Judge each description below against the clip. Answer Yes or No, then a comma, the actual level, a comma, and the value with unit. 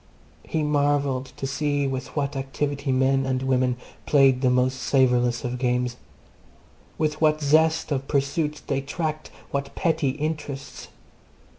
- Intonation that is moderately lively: No, narrow, 2.2 semitones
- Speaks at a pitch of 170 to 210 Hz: No, medium, 140 Hz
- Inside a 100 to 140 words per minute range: Yes, slow, 135 wpm